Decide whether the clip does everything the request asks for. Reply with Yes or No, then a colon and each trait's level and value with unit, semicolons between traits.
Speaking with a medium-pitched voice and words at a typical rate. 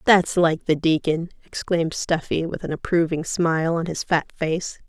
Yes: medium, 165 Hz; average, 170 wpm